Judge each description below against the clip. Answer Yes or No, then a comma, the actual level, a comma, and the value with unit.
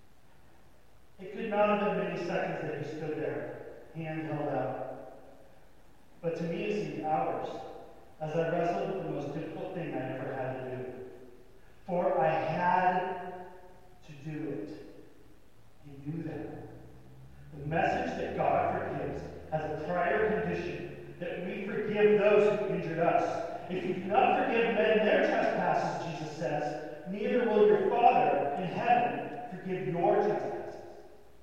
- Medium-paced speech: Yes, average, 145 wpm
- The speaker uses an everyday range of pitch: Yes, average, 4.0 semitones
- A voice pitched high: No, medium, 165 Hz